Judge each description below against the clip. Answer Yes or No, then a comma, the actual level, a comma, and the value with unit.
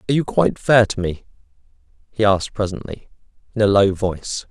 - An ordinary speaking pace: Yes, average, 175 wpm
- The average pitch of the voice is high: No, low, 105 Hz